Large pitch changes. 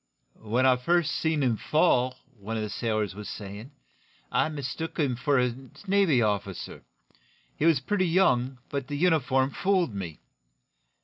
Yes: wide, 6.1 semitones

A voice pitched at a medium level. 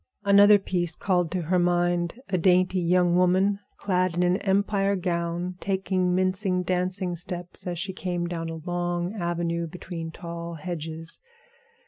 Yes: medium, 180 Hz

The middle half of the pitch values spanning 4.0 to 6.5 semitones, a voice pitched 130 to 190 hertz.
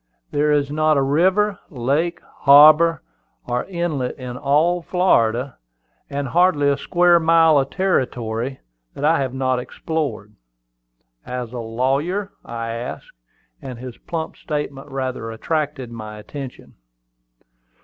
Yes: average, 4.5 semitones; medium, 140 Hz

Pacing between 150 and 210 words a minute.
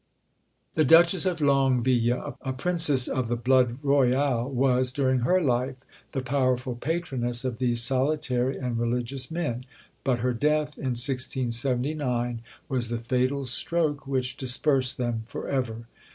No: average, 140 wpm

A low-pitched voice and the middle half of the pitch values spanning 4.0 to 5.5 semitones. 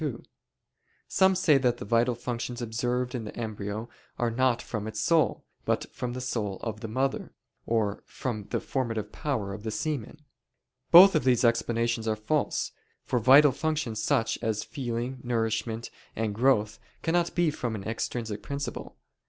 No: low, 120 Hz; average, 3.1 semitones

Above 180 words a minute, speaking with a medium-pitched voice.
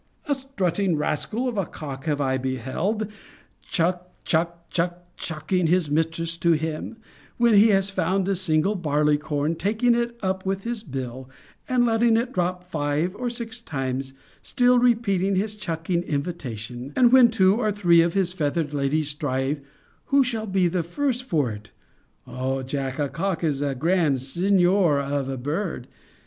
No: average, 165 wpm; medium, 170 Hz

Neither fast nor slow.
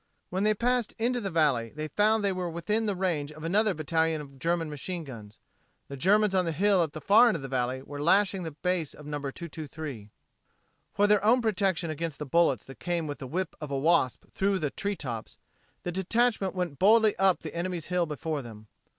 No: fast, 215 wpm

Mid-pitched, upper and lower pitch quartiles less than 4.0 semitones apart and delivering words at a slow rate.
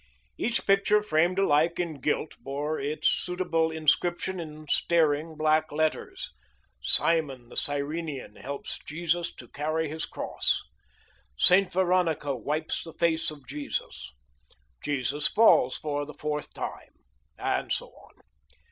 Yes: medium, 155 Hz; narrow, 2.6 semitones; slow, 125 wpm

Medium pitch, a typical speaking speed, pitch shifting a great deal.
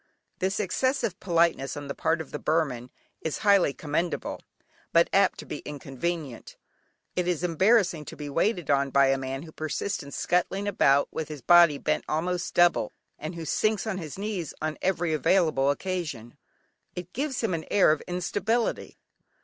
No: medium, 170 Hz; average, 170 wpm; average, 4.4 semitones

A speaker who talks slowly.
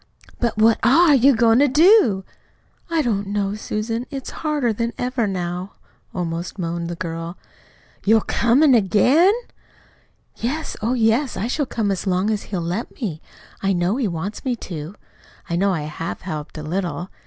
No: average, 165 wpm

